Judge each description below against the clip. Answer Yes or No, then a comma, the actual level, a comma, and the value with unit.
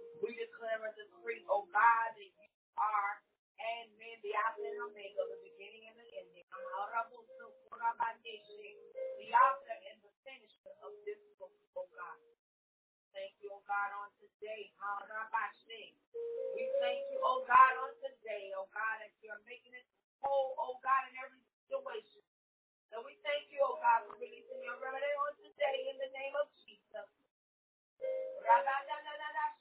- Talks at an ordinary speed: Yes, average, 165 wpm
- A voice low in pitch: No, very high, 275 Hz